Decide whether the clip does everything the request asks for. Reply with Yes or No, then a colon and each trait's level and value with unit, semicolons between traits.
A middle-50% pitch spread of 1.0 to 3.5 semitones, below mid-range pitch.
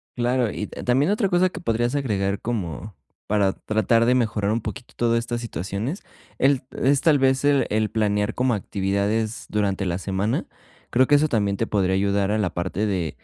No: average, 4.0 semitones; low, 110 Hz